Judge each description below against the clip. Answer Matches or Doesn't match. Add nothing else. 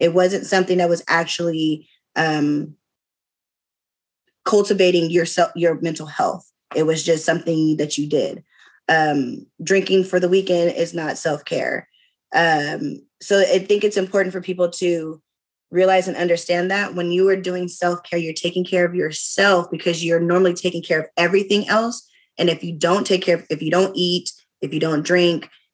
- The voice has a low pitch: Doesn't match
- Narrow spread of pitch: Matches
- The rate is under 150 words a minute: Doesn't match